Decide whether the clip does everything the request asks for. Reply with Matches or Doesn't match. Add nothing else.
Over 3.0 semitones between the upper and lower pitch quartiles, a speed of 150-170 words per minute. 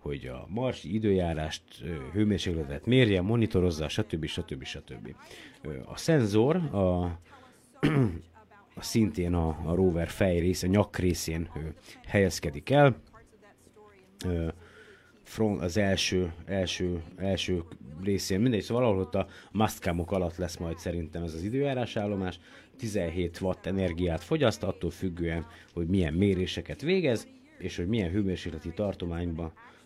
Doesn't match